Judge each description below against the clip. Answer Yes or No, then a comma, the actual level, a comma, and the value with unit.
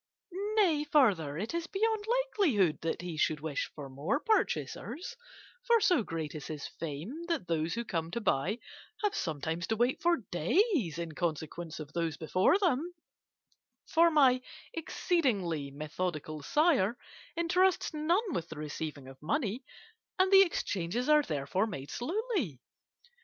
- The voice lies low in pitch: No, high, 210 Hz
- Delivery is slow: No, average, 145 wpm